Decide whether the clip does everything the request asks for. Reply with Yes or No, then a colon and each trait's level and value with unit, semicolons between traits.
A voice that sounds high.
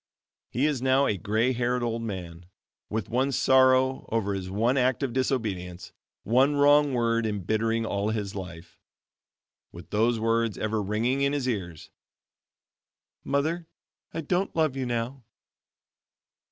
No: low, 115 Hz